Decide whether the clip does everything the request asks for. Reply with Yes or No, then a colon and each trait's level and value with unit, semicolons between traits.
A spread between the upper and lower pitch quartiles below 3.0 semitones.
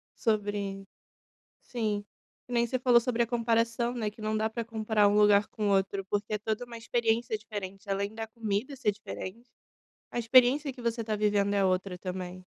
Yes: narrow, 2.5 semitones